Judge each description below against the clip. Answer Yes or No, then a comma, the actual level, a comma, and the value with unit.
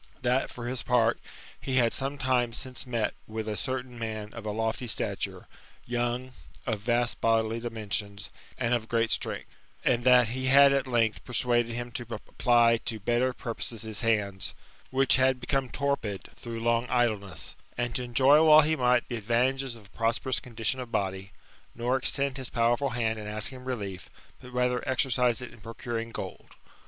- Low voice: Yes, low, 120 Hz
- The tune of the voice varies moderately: No, narrow, 2.2 semitones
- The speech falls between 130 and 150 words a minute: No, average, 175 wpm